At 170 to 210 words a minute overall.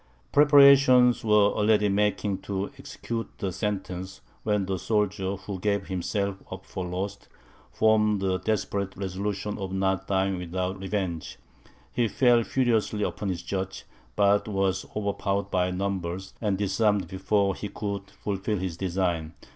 No: average, 140 wpm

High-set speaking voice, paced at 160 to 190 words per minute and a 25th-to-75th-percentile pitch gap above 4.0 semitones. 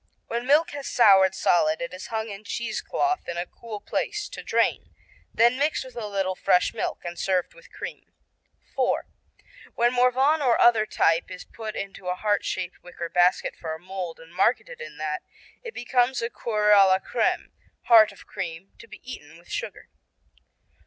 Yes: high, 210 Hz; average, 180 wpm; average, 5.3 semitones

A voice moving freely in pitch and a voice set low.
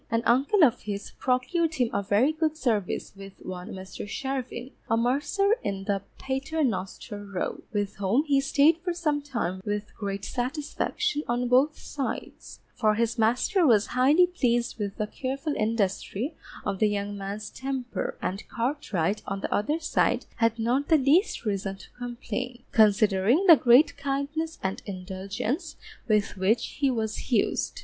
No: wide, 5.7 semitones; high, 240 Hz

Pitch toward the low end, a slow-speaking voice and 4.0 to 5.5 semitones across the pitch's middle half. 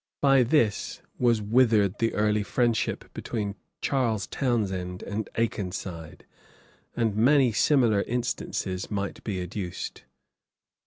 No: low, 110 Hz; slow, 105 wpm; average, 3.3 semitones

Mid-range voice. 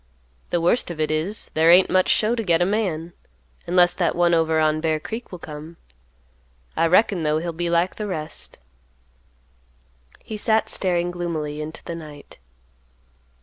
Yes: medium, 170 Hz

